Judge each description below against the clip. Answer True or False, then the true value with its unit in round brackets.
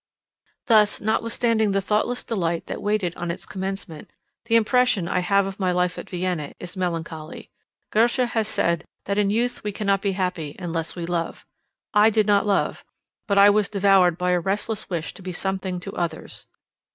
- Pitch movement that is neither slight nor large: True (3.0 semitones)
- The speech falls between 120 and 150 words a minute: False (180 wpm)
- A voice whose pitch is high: True (195 Hz)